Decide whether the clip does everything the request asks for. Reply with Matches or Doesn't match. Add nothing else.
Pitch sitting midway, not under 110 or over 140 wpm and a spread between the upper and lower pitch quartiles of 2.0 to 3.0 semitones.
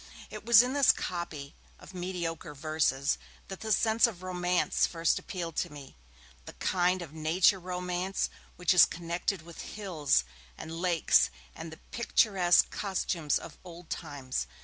Doesn't match